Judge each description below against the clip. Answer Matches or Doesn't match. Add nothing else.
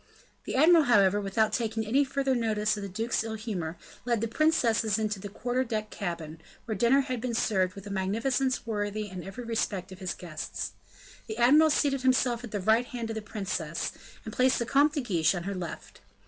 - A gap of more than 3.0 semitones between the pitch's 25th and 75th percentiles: Matches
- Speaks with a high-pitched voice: Matches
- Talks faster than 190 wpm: Matches